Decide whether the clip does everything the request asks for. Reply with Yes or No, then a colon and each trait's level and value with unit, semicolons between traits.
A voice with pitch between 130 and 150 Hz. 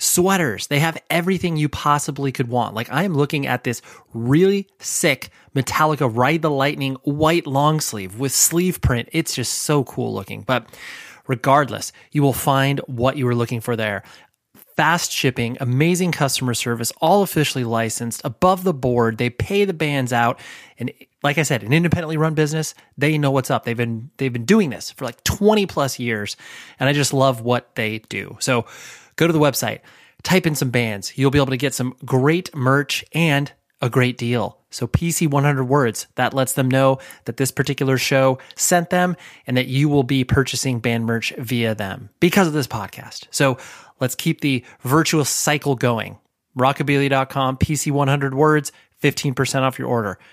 Yes: low, 135 Hz